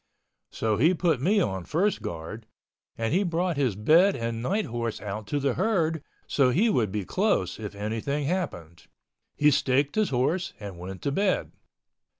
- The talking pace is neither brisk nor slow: Yes, average, 170 wpm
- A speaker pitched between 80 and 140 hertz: Yes, low, 135 Hz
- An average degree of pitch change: No, wide, 8.3 semitones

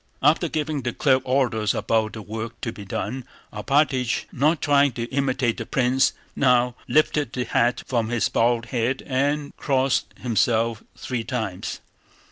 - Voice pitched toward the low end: Yes, low, 125 Hz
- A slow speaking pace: No, average, 150 wpm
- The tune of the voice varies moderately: Yes, average, 3.1 semitones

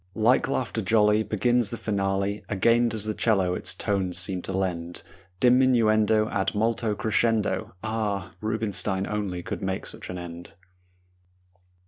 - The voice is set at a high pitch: No, low, 105 Hz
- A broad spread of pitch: No, average, 2.8 semitones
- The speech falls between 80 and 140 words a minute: Yes, slow, 135 wpm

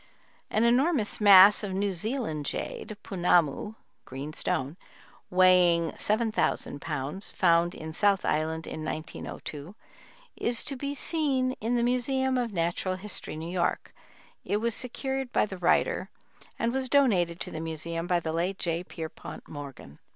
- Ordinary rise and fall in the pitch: No, wide, 6.2 semitones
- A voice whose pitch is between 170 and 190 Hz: Yes, medium, 185 Hz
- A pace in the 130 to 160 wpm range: Yes, average, 145 wpm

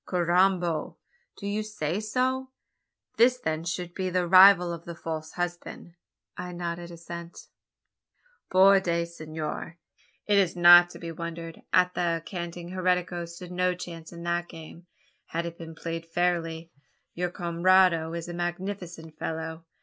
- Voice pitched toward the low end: No, medium, 175 Hz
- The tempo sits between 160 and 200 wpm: No, average, 150 wpm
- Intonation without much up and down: Yes, narrow, 1.5 semitones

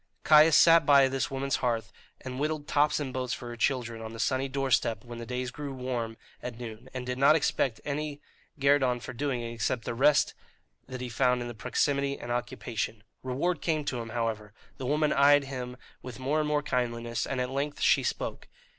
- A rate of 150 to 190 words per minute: No, fast, 205 wpm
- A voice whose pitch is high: No, low, 130 Hz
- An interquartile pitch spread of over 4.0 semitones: No, average, 3.0 semitones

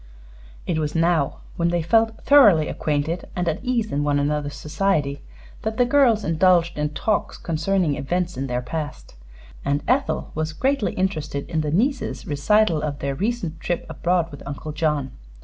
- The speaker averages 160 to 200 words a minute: Yes, average, 165 wpm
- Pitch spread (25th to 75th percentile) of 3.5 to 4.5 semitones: No, average, 5.0 semitones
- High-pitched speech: No, medium, 165 Hz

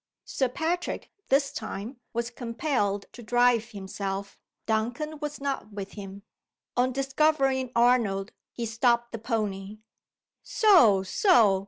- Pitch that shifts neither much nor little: Yes, average, 4.7 semitones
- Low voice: No, high, 235 Hz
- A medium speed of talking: No, slow, 120 wpm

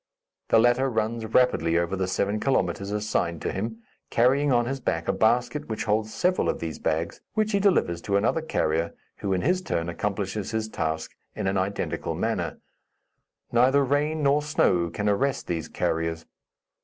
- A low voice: Yes, low, 110 Hz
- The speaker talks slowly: No, average, 170 wpm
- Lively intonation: Yes, wide, 7.0 semitones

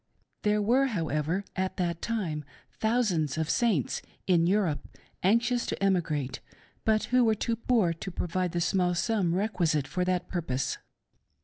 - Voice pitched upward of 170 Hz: Yes, medium, 185 Hz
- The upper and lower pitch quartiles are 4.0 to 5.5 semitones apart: Yes, average, 4.7 semitones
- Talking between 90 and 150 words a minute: Yes, average, 145 wpm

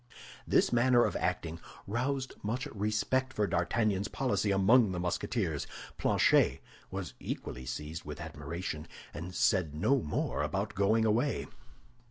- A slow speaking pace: Yes, slow, 130 wpm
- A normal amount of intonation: No, wide, 6.2 semitones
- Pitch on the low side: Yes, low, 100 Hz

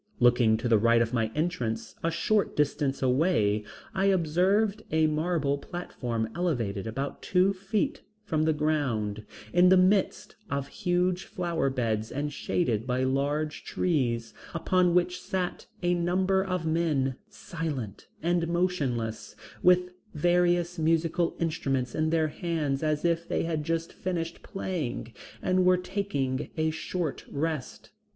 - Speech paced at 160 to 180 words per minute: No, average, 140 wpm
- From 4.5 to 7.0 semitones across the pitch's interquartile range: Yes, average, 5.2 semitones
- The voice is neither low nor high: Yes, medium, 160 Hz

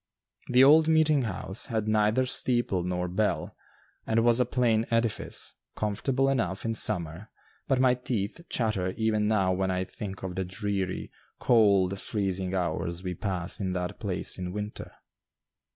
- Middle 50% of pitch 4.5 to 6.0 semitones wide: No, average, 4.1 semitones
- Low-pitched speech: Yes, low, 105 Hz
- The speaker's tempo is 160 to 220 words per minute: No, average, 150 wpm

